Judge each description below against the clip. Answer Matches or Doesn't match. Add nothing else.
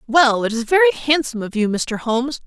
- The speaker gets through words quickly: Matches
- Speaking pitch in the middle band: Doesn't match